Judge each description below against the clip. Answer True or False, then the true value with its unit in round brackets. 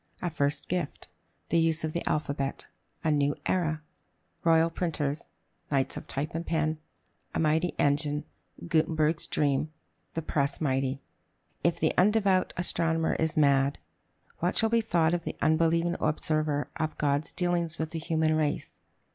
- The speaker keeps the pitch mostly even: True (2.2 semitones)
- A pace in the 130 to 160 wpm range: True (145 wpm)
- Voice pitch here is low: False (160 Hz)